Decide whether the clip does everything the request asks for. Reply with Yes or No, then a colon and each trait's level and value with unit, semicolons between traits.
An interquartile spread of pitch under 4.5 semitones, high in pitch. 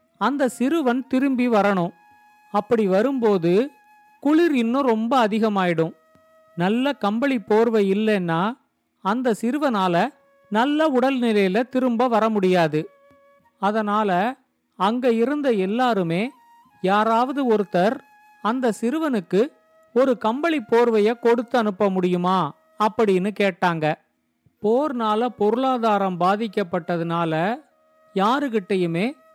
No: average, 5.0 semitones; high, 225 Hz